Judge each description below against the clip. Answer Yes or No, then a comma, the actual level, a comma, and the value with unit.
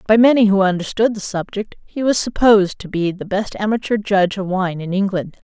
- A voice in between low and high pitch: No, high, 200 Hz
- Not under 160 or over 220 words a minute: Yes, fast, 205 wpm